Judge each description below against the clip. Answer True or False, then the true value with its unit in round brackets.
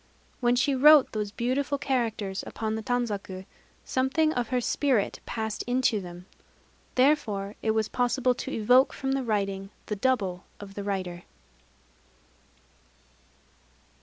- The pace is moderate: False (130 wpm)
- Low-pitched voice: False (225 Hz)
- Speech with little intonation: False (4.3 semitones)